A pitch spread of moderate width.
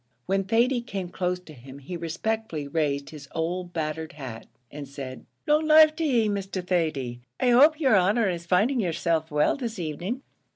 No: wide, 6.6 semitones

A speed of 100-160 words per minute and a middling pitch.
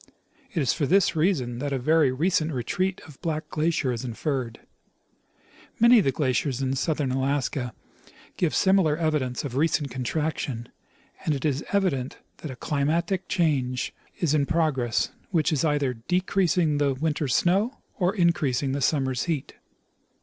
Yes: average, 150 wpm; medium, 150 Hz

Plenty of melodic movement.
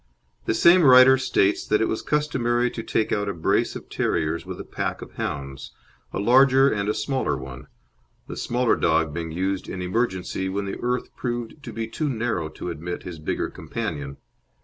Yes: wide, 6.7 semitones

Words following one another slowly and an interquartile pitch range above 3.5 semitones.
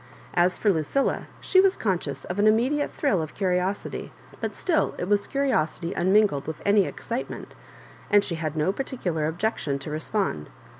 No: average, 165 wpm; wide, 5.4 semitones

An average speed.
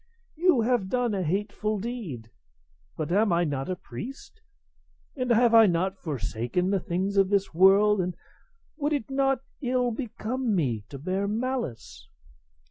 Yes: average, 150 wpm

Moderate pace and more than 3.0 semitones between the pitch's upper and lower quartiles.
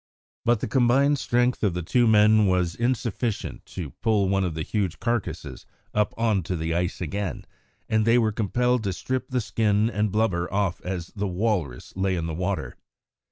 Yes: average, 185 wpm; average, 4.2 semitones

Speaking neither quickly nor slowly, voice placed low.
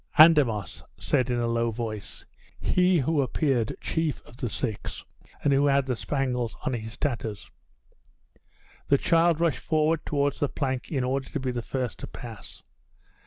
Yes: average, 160 wpm; low, 130 Hz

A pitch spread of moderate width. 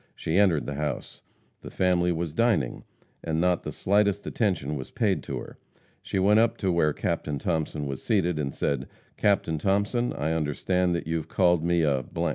Yes: average, 4.3 semitones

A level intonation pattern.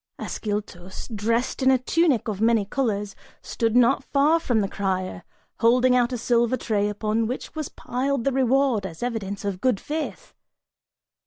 No: average, 4.0 semitones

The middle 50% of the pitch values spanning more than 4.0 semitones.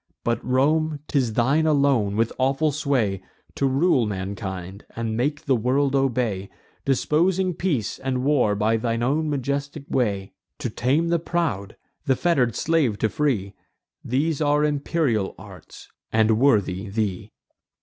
Yes: average, 5.2 semitones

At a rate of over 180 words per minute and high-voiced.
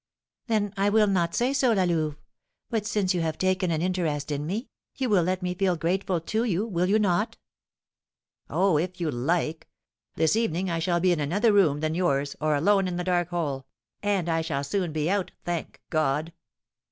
No: average, 200 wpm; medium, 175 Hz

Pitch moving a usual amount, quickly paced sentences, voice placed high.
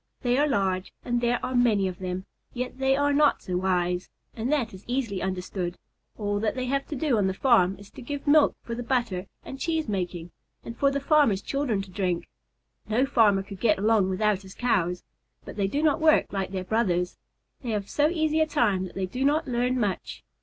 No: wide, 5.9 semitones; fast, 215 wpm; high, 220 Hz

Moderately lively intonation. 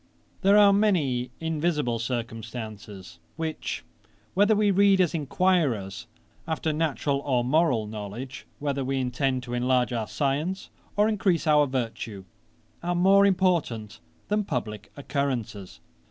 No: wide, 6.7 semitones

